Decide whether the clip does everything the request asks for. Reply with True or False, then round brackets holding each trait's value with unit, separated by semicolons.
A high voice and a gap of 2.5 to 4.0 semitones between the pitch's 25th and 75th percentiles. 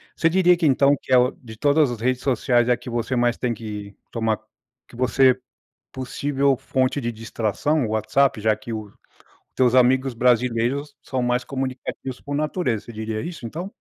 False (125 Hz; 3.2 semitones)